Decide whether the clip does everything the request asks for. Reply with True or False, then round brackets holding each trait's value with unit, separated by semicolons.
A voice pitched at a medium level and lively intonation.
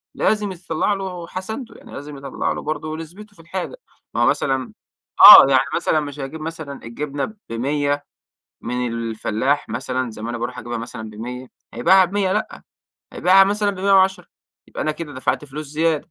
True (150 Hz; 6.4 semitones)